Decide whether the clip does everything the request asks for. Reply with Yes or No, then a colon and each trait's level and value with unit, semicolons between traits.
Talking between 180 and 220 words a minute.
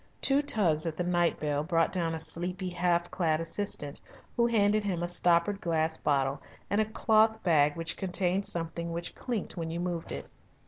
Yes: average, 185 wpm